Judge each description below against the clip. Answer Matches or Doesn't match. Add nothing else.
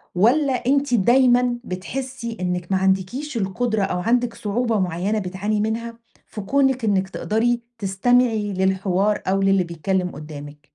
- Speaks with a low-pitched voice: Doesn't match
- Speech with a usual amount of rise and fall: Matches